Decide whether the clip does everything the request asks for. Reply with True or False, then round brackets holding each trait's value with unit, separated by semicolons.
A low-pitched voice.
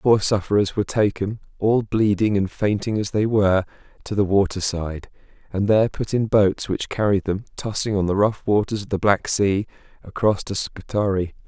True (100 Hz)